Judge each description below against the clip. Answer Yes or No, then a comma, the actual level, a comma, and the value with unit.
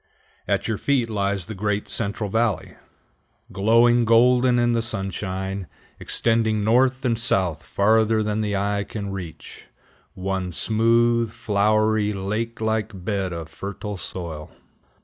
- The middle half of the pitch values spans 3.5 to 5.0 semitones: No, average, 2.8 semitones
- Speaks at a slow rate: Yes, slow, 130 wpm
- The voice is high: No, low, 105 Hz